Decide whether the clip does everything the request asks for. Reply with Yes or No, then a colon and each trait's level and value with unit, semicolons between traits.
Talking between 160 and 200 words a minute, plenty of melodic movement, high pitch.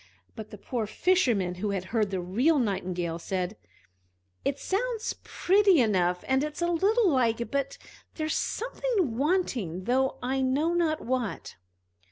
No: average, 145 wpm; wide, 9.0 semitones; very high, 260 Hz